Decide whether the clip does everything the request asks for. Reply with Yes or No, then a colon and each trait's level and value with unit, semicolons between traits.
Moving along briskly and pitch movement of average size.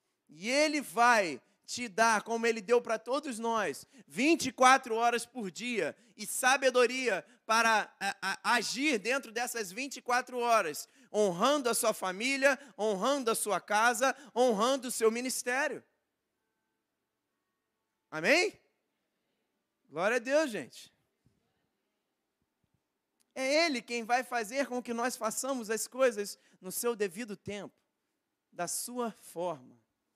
No: slow, 120 wpm; average, 3.1 semitones